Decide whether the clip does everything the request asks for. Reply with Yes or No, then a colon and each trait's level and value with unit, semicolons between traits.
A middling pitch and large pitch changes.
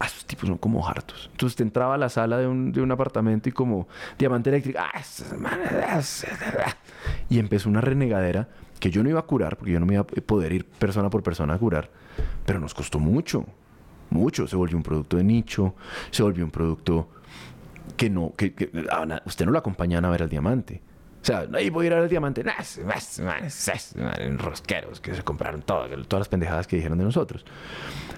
No: very low, 95 Hz; wide, 6.0 semitones